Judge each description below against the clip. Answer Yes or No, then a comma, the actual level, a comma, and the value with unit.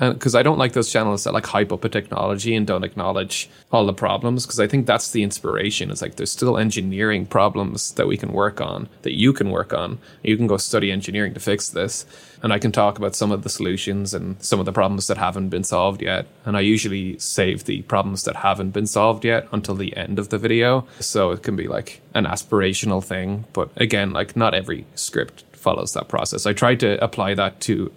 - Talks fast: Yes, fast, 230 wpm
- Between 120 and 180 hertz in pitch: No, low, 105 Hz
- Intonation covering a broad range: No, average, 2.8 semitones